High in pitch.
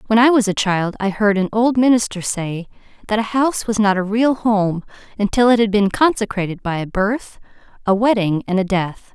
Yes: high, 210 Hz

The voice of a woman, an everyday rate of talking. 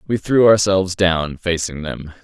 No: male; average, 160 wpm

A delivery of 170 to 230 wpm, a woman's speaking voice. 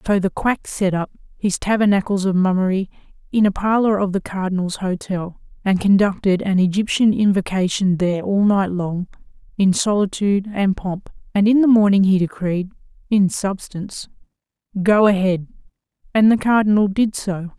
No: average, 150 wpm; female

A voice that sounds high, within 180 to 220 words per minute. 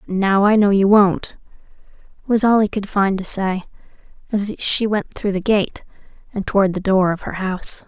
Yes: high, 200 Hz; average, 190 wpm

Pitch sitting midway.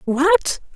No: very high, 270 Hz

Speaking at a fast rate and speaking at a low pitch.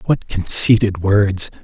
No: slow, 110 wpm; low, 100 Hz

